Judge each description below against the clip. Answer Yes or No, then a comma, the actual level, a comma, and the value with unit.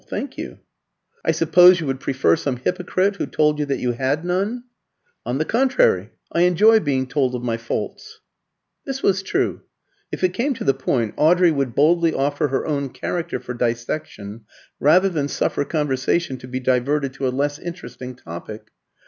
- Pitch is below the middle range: No, medium, 145 Hz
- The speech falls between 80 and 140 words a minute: No, average, 175 wpm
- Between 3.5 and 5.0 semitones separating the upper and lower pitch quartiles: No, wide, 5.4 semitones